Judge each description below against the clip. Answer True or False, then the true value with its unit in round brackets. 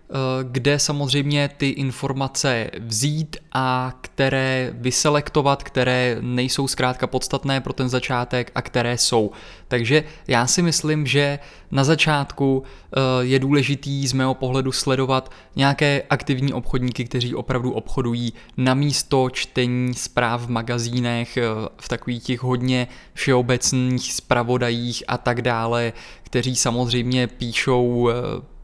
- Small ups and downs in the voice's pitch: True (2.0 semitones)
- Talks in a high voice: False (130 Hz)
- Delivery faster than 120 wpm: False (115 wpm)